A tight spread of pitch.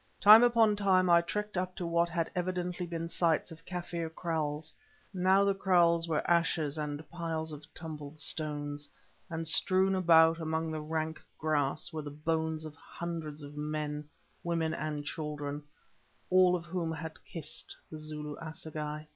Yes: narrow, 2.3 semitones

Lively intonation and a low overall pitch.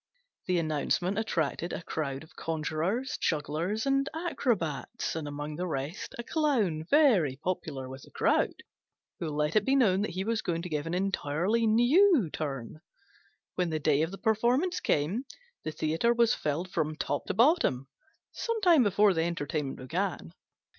No: wide, 6.9 semitones; medium, 175 Hz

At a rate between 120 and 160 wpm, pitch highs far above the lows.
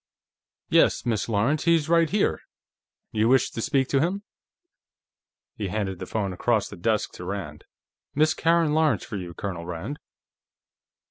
Yes: average, 150 wpm; wide, 7.8 semitones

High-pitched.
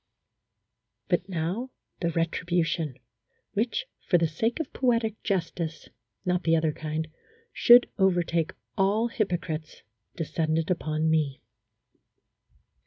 No: medium, 170 Hz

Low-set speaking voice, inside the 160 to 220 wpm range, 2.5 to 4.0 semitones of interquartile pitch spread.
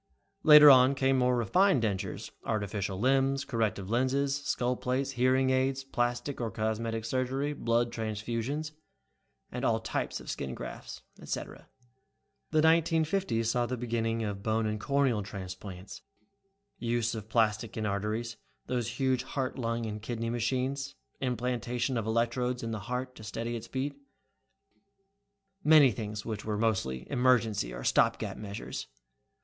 No: low, 120 Hz; average, 140 wpm; average, 3.2 semitones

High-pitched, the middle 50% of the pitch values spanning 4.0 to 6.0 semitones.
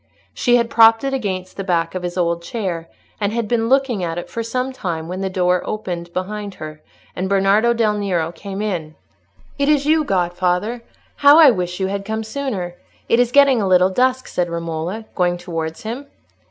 Yes: high, 195 Hz; average, 4.8 semitones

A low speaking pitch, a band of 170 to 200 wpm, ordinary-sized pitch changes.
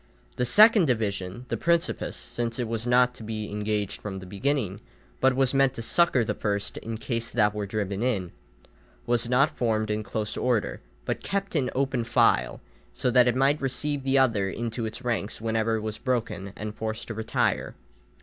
Yes: low, 115 Hz; average, 190 wpm; average, 3.2 semitones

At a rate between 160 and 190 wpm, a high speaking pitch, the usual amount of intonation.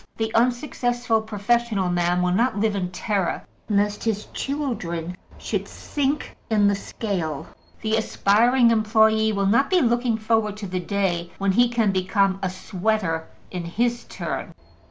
No: average, 150 wpm; high, 215 Hz; average, 3.7 semitones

